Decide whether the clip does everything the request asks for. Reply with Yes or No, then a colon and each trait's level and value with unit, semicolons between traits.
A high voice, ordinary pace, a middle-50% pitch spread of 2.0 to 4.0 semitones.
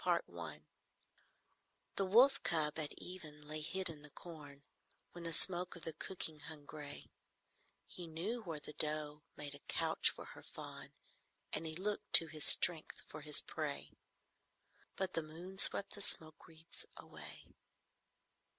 No: medium, 160 Hz; average, 155 wpm; average, 3.2 semitones